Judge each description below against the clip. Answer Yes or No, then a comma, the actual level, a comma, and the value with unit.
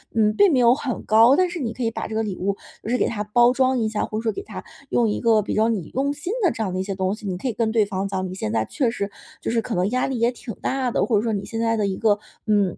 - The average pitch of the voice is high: Yes, high, 225 Hz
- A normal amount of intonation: Yes, average, 3.4 semitones